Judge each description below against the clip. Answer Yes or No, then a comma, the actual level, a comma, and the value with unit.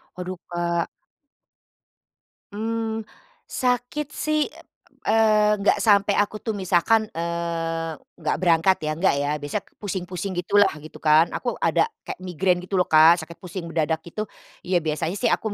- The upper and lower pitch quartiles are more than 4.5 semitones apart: No, average, 3.9 semitones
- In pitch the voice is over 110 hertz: Yes, medium, 185 Hz